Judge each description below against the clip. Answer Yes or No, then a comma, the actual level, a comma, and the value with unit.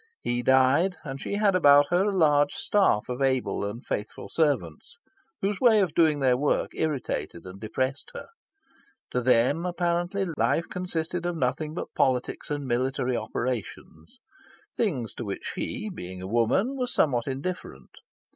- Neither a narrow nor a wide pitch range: No, wide, 6.2 semitones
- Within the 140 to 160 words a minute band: Yes, average, 155 wpm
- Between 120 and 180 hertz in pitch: Yes, medium, 140 Hz